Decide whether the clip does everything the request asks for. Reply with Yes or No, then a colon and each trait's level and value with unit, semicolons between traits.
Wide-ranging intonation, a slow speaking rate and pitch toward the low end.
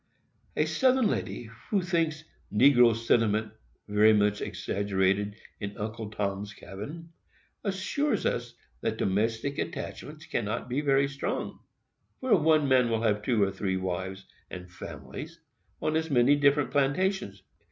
Yes: wide, 6.6 semitones; slow, 130 wpm; low, 115 Hz